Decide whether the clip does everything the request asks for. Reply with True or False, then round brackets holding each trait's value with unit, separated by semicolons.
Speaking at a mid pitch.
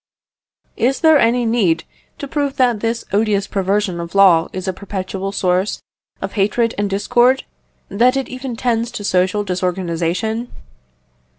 False (205 Hz)